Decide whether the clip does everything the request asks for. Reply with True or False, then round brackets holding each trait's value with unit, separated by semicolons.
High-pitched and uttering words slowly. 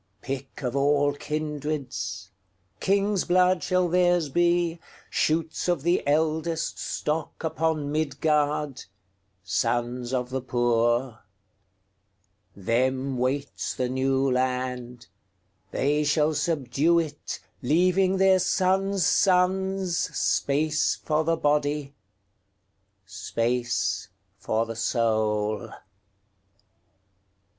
False (140 Hz; 70 wpm)